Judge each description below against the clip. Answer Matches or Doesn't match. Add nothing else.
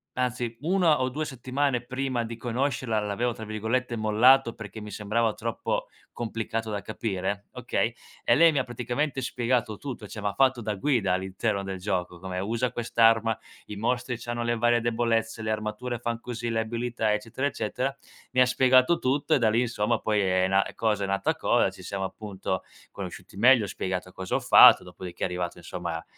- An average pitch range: Matches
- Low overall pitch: Matches